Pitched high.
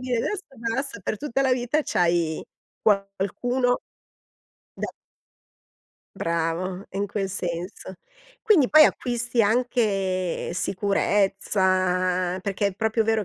Yes: high, 200 Hz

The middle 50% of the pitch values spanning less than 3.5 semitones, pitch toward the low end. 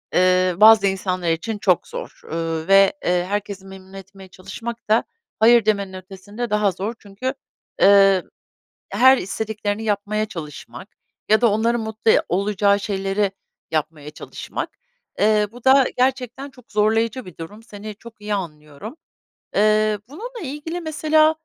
No: average, 3.0 semitones; high, 210 Hz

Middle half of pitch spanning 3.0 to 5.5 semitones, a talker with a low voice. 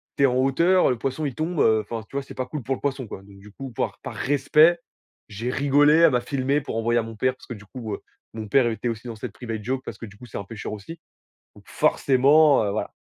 Yes: average, 4.0 semitones; low, 125 Hz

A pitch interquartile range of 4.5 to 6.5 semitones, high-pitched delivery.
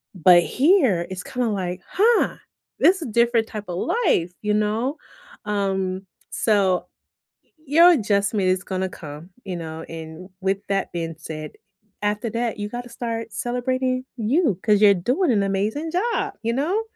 Yes: average, 5.1 semitones; high, 210 Hz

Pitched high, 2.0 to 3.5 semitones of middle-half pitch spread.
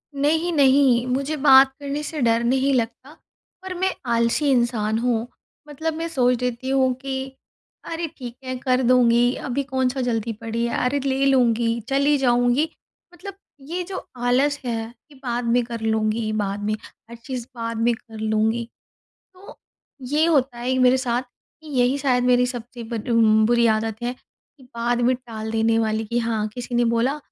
Yes: high, 245 Hz; average, 2.7 semitones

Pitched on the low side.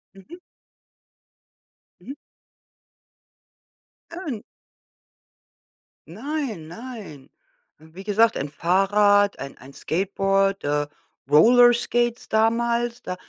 No: high, 205 Hz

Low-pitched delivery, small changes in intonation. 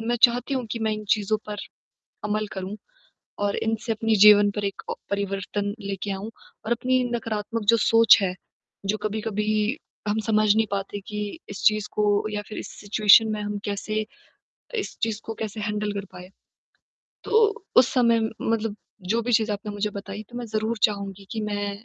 No: high, 215 Hz; narrow, 1.6 semitones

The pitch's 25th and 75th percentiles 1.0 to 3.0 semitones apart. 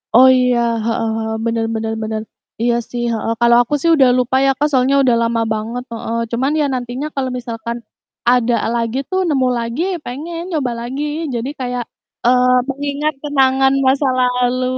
Yes: narrow, 2.4 semitones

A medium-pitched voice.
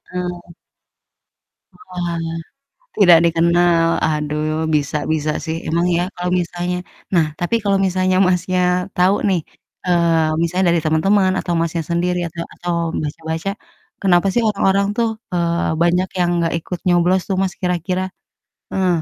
Yes: medium, 175 Hz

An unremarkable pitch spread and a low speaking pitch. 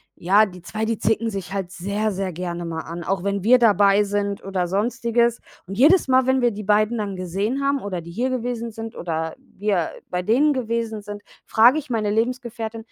No: average, 3.4 semitones; high, 210 Hz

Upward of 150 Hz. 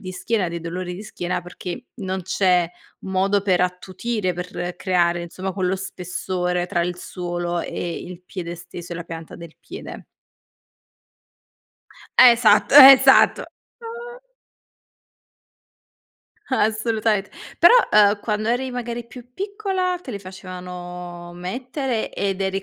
Yes: high, 190 Hz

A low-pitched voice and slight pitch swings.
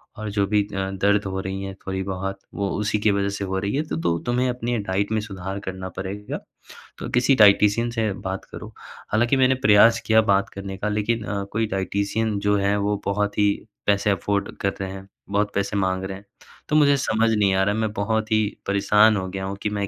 Yes: low, 100 Hz; narrow, 1.9 semitones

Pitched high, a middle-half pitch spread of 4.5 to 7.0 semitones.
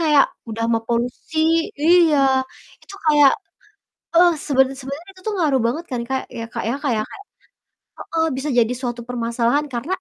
Yes: very high, 270 Hz; average, 4.8 semitones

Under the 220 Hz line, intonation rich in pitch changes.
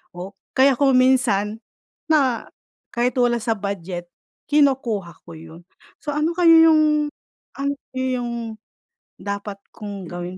No: high, 235 Hz; wide, 5.8 semitones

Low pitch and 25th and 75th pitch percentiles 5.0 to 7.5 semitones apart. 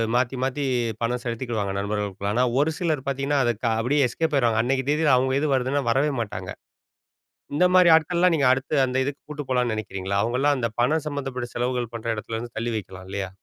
No: low, 125 Hz; average, 3.9 semitones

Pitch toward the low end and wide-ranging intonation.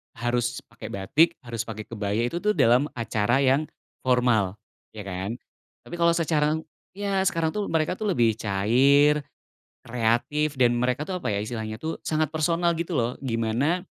Yes: low, 130 Hz; wide, 6.1 semitones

